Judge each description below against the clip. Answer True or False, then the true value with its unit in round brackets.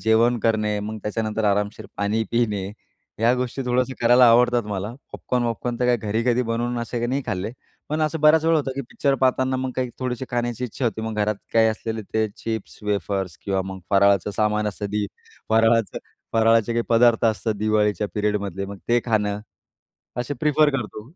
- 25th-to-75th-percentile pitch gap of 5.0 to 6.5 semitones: False (2.7 semitones)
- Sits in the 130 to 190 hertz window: False (115 Hz)